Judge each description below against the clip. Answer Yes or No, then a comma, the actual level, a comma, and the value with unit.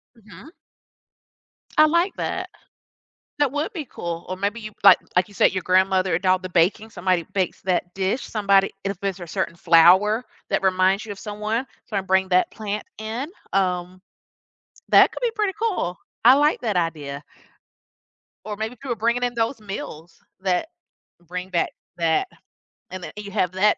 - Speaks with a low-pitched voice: No, high, 195 Hz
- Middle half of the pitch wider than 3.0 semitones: Yes, average, 3.7 semitones